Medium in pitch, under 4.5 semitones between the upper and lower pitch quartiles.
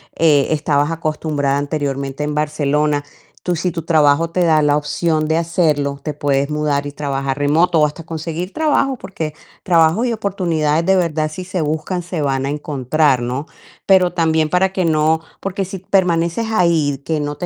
Yes: medium, 155 Hz; average, 2.9 semitones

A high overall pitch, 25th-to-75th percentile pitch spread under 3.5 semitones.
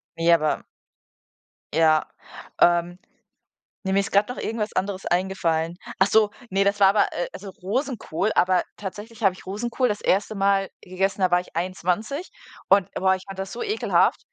Yes: high, 195 Hz; narrow, 2.5 semitones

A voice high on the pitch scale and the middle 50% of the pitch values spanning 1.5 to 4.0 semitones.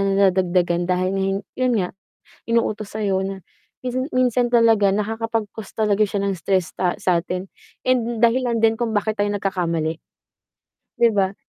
Yes: high, 205 Hz; average, 3.2 semitones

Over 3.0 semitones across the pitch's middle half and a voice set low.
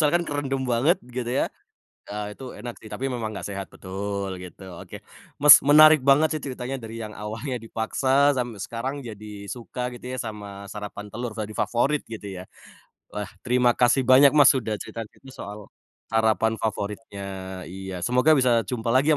Yes: average, 4.2 semitones; low, 115 Hz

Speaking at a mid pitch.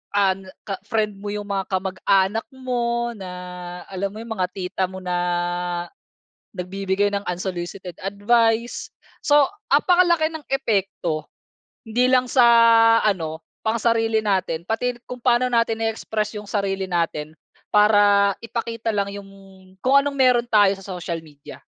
No: high, 205 Hz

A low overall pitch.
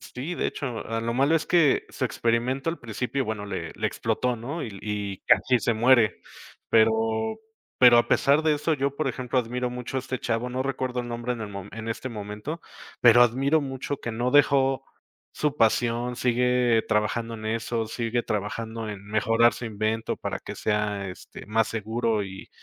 Yes: low, 120 Hz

